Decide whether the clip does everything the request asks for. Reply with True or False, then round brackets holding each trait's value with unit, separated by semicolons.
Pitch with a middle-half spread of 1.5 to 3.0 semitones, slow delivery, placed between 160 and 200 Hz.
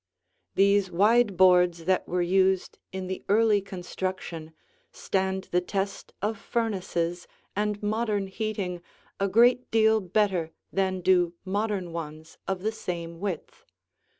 True (2.7 semitones; 125 wpm; 190 Hz)